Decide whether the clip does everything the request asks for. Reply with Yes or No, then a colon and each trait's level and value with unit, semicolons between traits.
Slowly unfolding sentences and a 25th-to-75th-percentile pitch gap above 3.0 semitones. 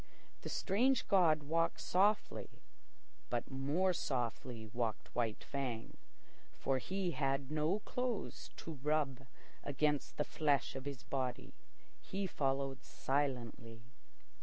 Yes: slow, 110 wpm; average, 4.2 semitones